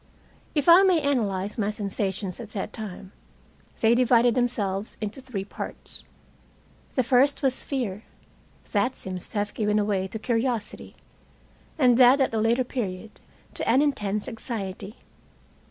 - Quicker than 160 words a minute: No, average, 140 wpm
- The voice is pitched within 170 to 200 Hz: No, high, 220 Hz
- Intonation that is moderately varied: Yes, average, 3.9 semitones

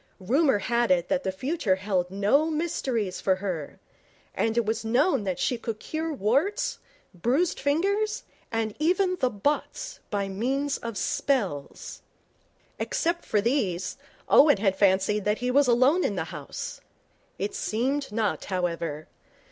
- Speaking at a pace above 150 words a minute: No, average, 145 wpm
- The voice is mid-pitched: No, high, 230 Hz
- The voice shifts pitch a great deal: Yes, wide, 6.7 semitones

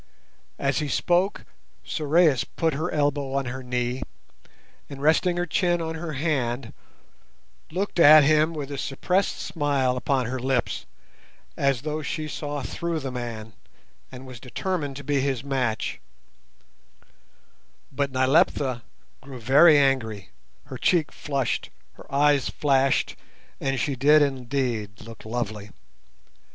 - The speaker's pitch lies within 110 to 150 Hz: Yes, medium, 140 Hz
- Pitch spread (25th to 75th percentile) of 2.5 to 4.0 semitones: Yes, average, 3.1 semitones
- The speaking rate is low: Yes, slow, 130 wpm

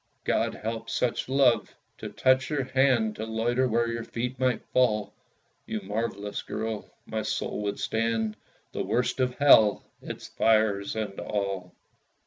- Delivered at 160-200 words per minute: No, average, 145 wpm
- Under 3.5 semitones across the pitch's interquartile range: Yes, average, 2.8 semitones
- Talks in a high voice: No, low, 115 Hz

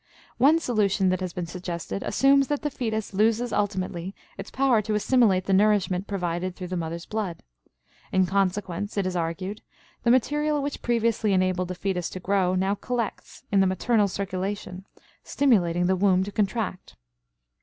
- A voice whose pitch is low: No, high, 195 Hz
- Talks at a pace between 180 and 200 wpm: No, average, 165 wpm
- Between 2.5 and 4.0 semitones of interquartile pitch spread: Yes, average, 3.2 semitones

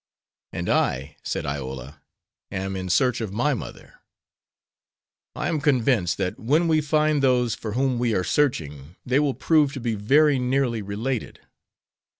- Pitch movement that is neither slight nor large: No, wide, 6.6 semitones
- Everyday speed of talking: Yes, average, 155 wpm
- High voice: No, low, 120 Hz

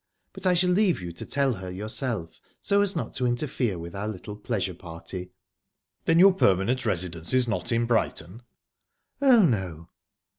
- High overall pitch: No, low, 110 Hz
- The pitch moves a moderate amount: No, wide, 8.0 semitones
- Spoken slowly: No, average, 170 wpm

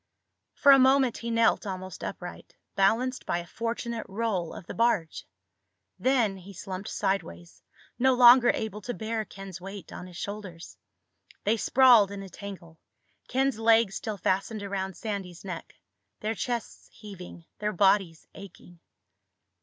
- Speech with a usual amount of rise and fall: Yes, average, 3.6 semitones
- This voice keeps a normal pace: Yes, average, 145 wpm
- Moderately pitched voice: No, high, 200 Hz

